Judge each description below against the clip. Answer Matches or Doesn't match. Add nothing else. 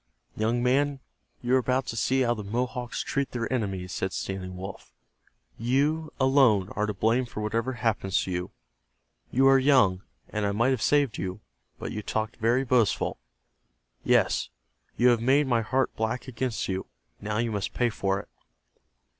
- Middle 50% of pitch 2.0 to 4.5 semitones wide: Matches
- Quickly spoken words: Doesn't match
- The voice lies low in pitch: Matches